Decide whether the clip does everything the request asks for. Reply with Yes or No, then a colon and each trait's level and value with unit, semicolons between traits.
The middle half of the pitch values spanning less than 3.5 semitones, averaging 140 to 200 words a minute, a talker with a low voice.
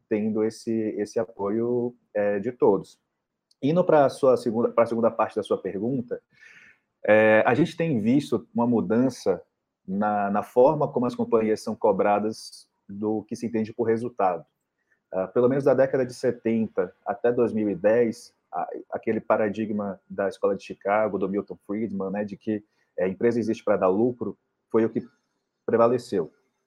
Yes: narrow, 2.4 semitones; average, 155 wpm; low, 110 Hz